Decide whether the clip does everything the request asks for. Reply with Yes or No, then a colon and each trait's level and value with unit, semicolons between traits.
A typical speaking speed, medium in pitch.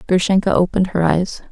Yes: average, 160 wpm; medium, 180 Hz